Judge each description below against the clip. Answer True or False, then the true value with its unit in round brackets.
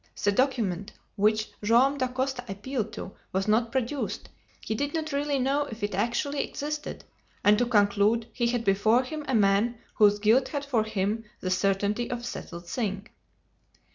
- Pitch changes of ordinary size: True (4.4 semitones)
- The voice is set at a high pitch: True (230 Hz)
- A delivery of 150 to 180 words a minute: True (170 wpm)